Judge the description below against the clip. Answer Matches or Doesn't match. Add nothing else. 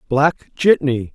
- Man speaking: Matches